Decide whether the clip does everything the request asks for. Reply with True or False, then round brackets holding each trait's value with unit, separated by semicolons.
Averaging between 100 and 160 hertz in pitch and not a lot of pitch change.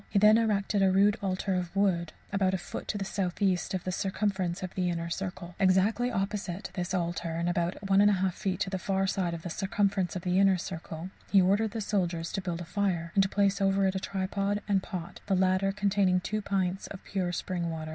False (190 Hz; 1.9 semitones)